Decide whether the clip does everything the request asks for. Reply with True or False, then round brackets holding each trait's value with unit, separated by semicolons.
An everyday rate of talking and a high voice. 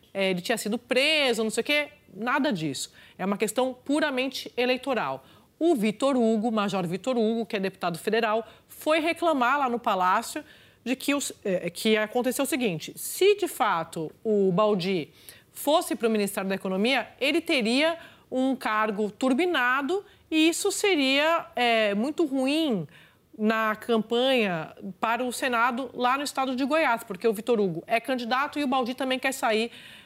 True (160 wpm; 245 Hz)